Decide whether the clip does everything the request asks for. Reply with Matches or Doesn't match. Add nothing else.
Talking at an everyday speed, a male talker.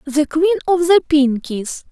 Doesn't match